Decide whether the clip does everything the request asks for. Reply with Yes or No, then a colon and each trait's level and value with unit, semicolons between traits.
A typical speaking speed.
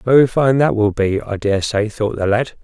No: fast, 250 wpm